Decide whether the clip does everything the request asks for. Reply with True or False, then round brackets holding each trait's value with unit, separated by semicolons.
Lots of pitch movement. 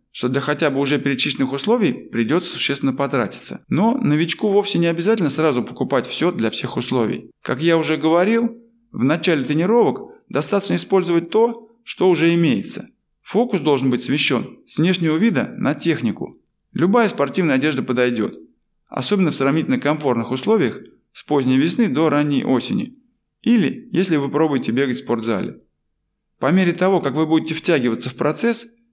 True (7.0 semitones)